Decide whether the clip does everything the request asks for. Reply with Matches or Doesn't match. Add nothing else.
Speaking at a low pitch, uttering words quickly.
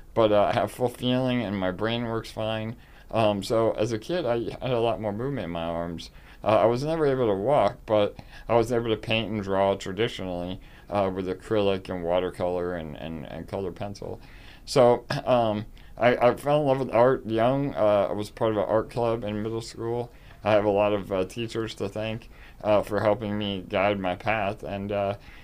Matches